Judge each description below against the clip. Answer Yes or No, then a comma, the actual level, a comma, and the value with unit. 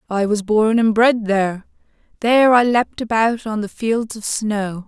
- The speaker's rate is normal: Yes, average, 170 wpm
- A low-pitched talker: No, high, 220 Hz